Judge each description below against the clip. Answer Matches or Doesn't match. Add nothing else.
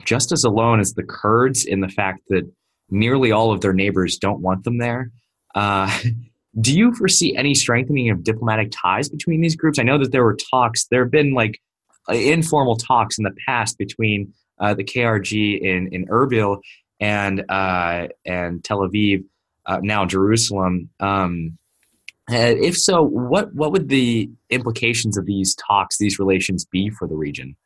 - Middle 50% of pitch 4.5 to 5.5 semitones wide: Doesn't match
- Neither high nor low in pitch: Doesn't match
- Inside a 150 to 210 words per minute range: Matches